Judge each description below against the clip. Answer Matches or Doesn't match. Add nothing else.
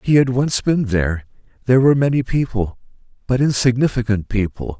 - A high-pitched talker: Doesn't match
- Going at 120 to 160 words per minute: Matches